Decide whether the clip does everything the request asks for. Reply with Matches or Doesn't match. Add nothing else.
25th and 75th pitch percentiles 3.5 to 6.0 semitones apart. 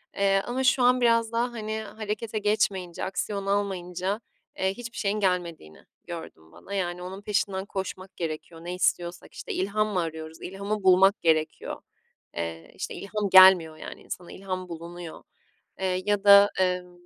Doesn't match